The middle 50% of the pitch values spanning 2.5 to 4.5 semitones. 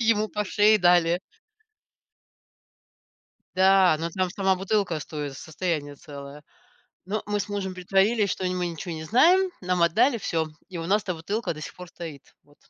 Yes: average, 3.9 semitones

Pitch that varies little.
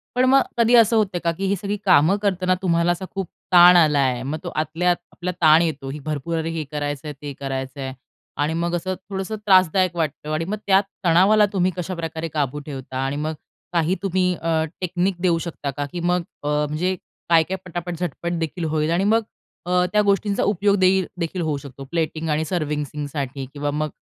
No: average, 3.7 semitones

